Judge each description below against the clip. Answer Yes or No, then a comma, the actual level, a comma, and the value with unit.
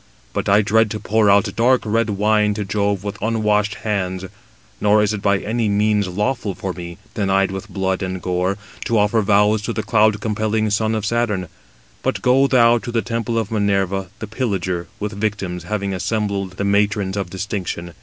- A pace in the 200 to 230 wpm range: No, average, 185 wpm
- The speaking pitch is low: Yes, low, 105 Hz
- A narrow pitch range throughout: Yes, narrow, 2.0 semitones